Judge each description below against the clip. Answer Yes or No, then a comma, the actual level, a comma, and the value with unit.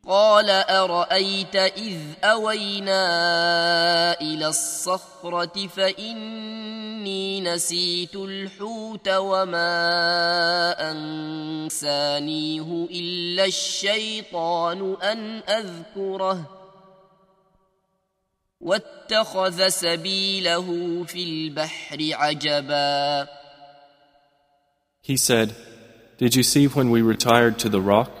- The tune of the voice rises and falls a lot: No, average, 3.9 semitones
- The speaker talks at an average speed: No, slow, 50 wpm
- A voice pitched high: No, medium, 175 Hz